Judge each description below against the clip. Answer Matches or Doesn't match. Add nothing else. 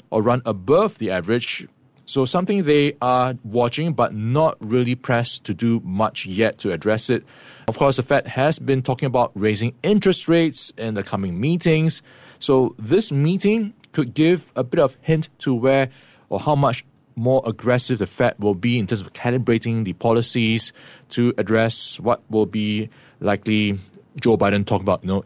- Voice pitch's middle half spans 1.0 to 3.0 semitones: Doesn't match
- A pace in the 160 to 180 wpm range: Matches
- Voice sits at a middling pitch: Doesn't match